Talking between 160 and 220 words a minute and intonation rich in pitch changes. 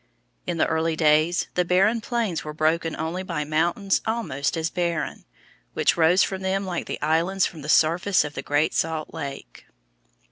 No: average, 175 wpm; average, 3.2 semitones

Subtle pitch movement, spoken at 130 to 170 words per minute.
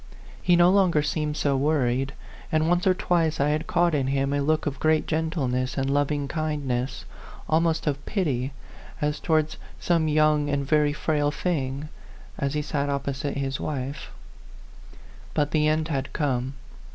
Yes: narrow, 2.2 semitones; average, 165 wpm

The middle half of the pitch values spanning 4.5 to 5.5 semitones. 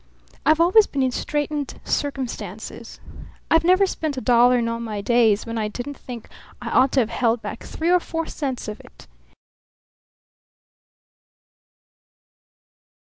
Yes: average, 4.8 semitones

